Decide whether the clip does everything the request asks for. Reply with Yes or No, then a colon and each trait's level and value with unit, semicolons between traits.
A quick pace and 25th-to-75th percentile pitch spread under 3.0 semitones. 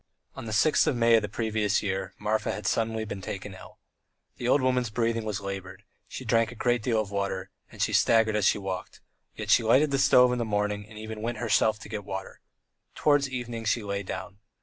Yes: fast, 220 wpm; narrow, 2.5 semitones